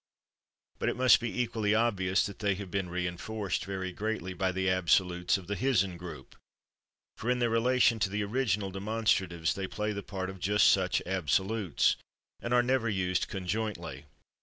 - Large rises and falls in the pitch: No, average, 3.2 semitones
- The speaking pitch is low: Yes, low, 100 Hz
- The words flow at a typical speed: Yes, average, 170 wpm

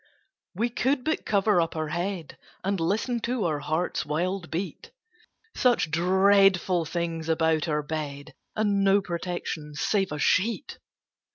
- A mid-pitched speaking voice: Yes, medium, 180 Hz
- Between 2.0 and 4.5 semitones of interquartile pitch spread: Yes, average, 4.0 semitones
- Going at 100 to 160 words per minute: Yes, average, 140 wpm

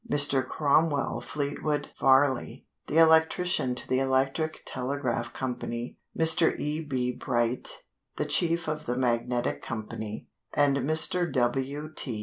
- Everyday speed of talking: No, slow, 130 wpm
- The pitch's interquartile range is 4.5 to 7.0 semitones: No, average, 3.7 semitones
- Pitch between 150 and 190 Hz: No, low, 135 Hz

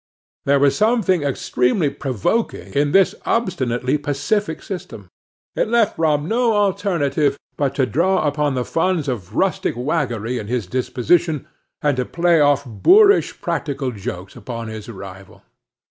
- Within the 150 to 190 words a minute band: No, average, 140 wpm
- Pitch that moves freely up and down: Yes, wide, 6.1 semitones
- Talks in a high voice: No, medium, 145 Hz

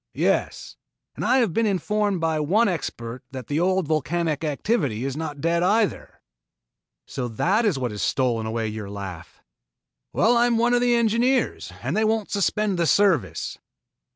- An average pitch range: No, wide, 8.7 semitones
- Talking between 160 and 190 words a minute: Yes, average, 170 wpm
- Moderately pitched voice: Yes, medium, 170 Hz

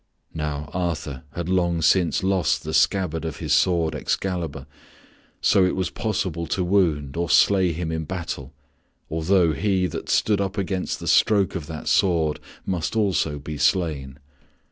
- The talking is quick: No, average, 155 wpm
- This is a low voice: Yes, very low, 85 Hz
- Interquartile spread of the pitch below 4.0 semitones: Yes, average, 3.2 semitones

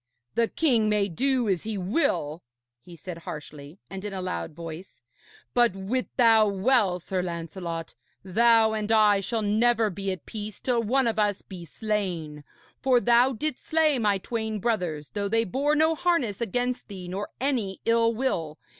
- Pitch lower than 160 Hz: No, high, 210 Hz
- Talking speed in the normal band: Yes, average, 170 wpm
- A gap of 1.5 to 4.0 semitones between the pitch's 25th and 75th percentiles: No, average, 4.5 semitones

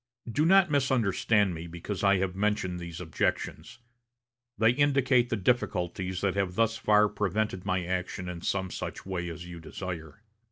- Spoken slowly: No, average, 160 wpm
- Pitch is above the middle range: No, very low, 95 Hz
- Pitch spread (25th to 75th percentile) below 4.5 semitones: Yes, average, 3.8 semitones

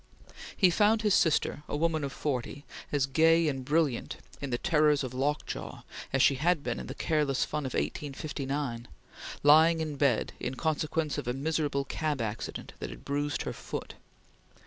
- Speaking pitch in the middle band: Yes, medium, 145 Hz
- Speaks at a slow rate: No, average, 170 wpm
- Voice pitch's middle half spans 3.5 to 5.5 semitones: No, average, 2.9 semitones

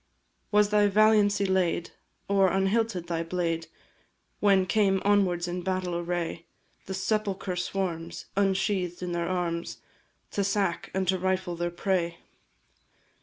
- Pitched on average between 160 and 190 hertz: Yes, medium, 185 Hz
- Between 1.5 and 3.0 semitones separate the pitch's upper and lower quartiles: Yes, narrow, 2.4 semitones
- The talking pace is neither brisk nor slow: No, slow, 125 wpm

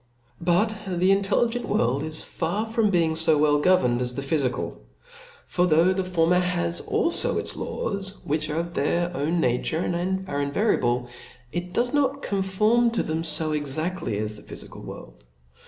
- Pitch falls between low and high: Yes, medium, 170 Hz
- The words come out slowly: No, average, 155 wpm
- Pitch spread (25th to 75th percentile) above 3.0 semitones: Yes, average, 4.7 semitones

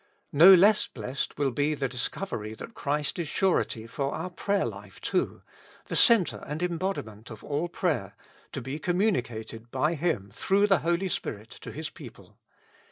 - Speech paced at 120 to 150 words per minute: No, average, 165 wpm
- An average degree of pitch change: No, wide, 7.2 semitones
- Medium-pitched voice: Yes, medium, 150 Hz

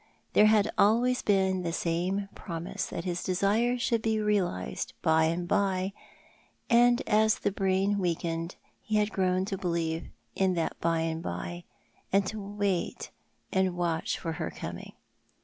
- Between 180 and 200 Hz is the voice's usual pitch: Yes, high, 190 Hz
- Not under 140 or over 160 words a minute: Yes, average, 155 wpm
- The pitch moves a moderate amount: Yes, average, 3.5 semitones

